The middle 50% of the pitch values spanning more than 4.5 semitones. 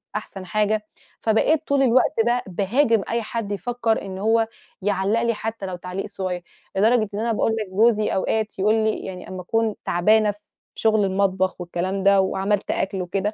No: average, 2.8 semitones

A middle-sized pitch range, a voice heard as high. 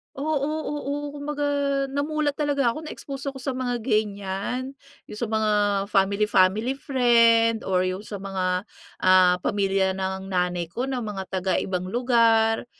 No: wide, 5.7 semitones; high, 225 Hz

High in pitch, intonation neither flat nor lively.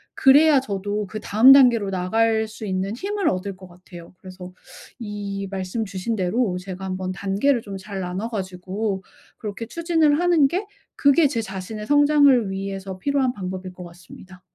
Yes: high, 205 Hz; average, 5.0 semitones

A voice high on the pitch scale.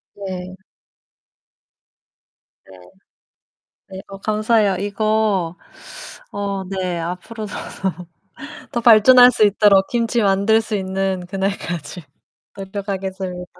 Yes: high, 195 Hz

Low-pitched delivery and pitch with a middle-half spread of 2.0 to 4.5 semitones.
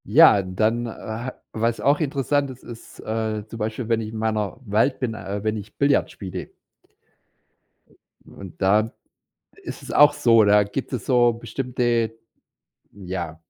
Yes: low, 110 Hz; narrow, 2.6 semitones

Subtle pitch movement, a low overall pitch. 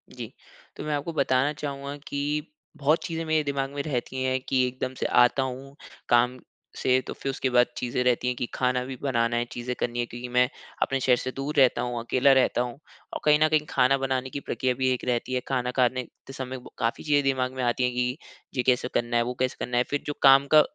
Yes: narrow, 1.9 semitones; low, 130 Hz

